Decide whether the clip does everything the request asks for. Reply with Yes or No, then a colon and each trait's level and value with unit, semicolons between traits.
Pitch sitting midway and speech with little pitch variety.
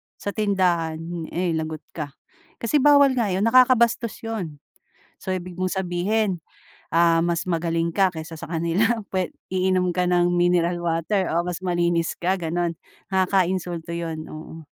Yes: medium, 175 Hz; narrow, 2.3 semitones